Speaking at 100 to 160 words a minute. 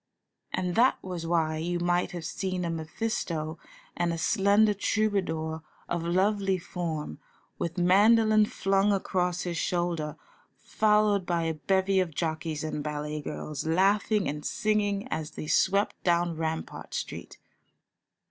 Yes: slow, 135 wpm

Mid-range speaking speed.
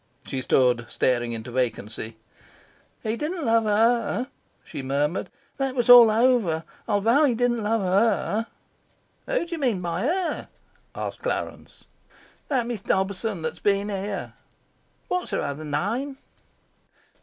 No: slow, 130 wpm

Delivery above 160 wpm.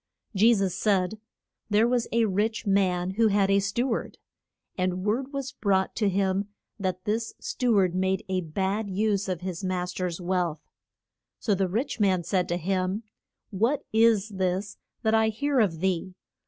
Yes: average, 170 wpm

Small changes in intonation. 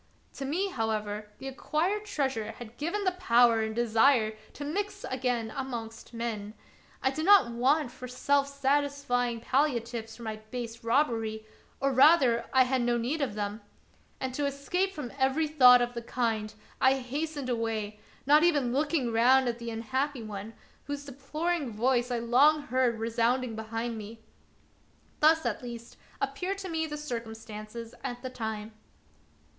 No: average, 3.8 semitones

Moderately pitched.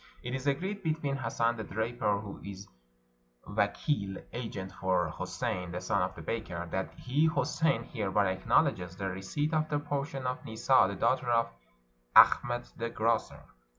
No: low, 115 Hz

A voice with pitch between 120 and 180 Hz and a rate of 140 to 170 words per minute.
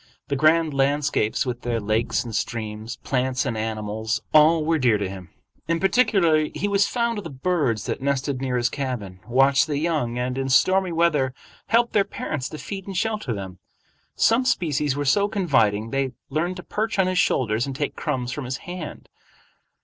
No: medium, 140 Hz; average, 190 wpm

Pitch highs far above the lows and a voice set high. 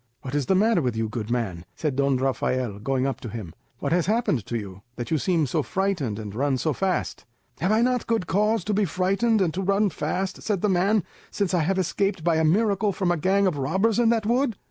No: wide, 7.3 semitones; medium, 180 Hz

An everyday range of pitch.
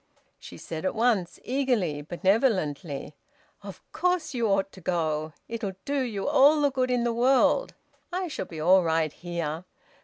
No: wide, 7.7 semitones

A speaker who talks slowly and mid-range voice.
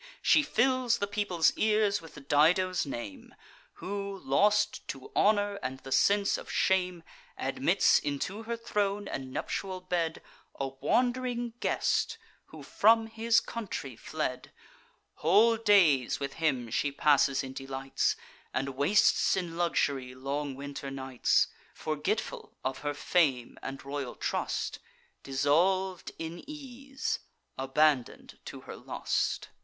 Yes: slow, 125 wpm; medium, 175 Hz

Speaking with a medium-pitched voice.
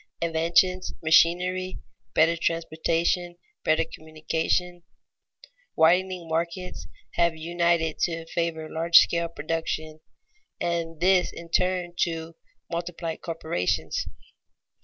Yes: medium, 170 Hz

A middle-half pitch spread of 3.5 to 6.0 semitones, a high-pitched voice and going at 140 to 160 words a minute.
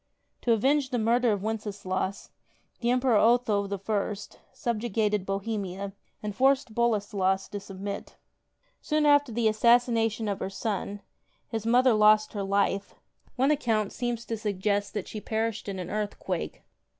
No: average, 2.8 semitones; high, 215 Hz; average, 145 wpm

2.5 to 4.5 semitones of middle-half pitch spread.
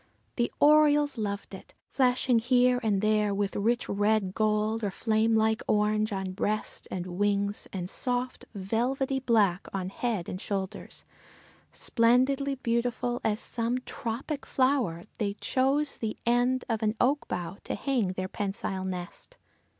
Yes: average, 3.7 semitones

